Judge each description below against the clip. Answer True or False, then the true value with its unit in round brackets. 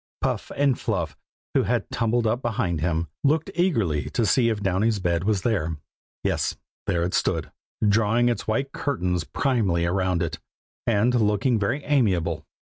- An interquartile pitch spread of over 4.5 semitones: True (5.5 semitones)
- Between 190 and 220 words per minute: False (155 wpm)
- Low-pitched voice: True (105 Hz)